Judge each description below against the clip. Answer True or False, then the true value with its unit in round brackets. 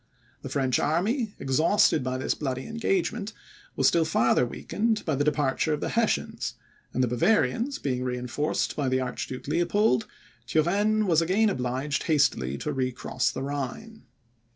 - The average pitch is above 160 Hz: False (150 Hz)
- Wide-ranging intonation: True (8.0 semitones)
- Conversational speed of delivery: True (150 wpm)